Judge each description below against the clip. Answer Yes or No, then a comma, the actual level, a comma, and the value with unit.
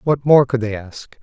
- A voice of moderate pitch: No, low, 125 Hz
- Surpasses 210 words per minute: Yes, fast, 245 wpm